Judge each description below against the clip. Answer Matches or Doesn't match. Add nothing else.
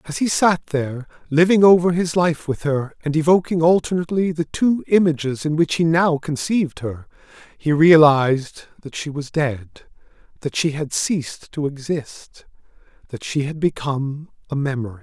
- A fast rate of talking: Doesn't match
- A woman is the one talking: Doesn't match